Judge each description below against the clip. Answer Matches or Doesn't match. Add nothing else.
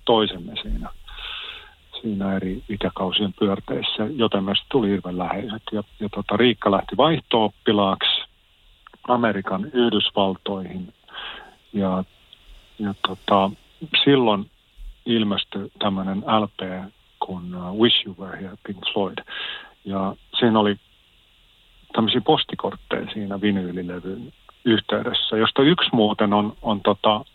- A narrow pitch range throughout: Matches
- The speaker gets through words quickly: Doesn't match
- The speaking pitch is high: Doesn't match